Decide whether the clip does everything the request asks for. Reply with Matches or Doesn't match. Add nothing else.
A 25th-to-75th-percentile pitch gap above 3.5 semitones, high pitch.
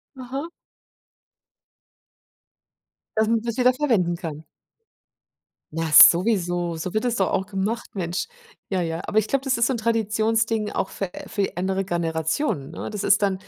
Matches